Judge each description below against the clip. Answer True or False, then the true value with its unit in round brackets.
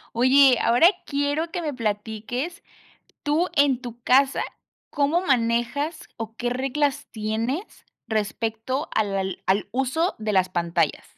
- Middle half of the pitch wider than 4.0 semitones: True (4.6 semitones)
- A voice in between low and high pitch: False (250 Hz)